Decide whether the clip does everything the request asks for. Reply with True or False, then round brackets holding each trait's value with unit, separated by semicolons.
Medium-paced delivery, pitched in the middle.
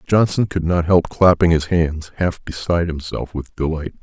False (180 wpm; 85 Hz)